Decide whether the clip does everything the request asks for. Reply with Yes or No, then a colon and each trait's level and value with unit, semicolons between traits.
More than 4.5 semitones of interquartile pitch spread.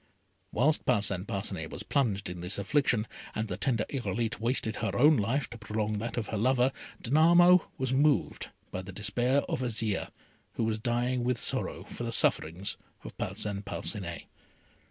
No: average, 4.1 semitones